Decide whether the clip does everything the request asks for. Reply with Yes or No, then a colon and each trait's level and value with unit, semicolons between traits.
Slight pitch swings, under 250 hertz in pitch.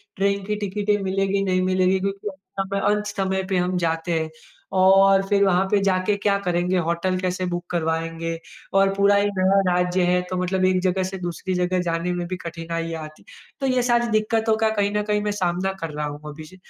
Yes: narrow, 2.1 semitones; medium, 185 Hz